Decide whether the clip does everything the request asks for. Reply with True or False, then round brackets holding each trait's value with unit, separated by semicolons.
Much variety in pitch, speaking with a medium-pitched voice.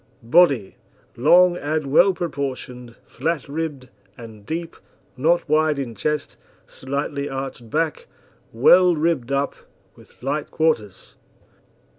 False (4.1 semitones; 145 Hz)